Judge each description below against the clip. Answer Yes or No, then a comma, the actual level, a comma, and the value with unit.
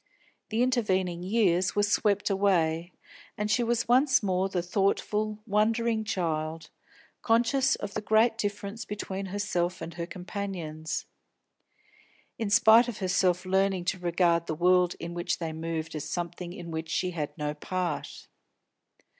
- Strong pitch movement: No, average, 3.5 semitones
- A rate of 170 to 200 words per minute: No, average, 145 wpm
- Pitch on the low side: No, medium, 185 Hz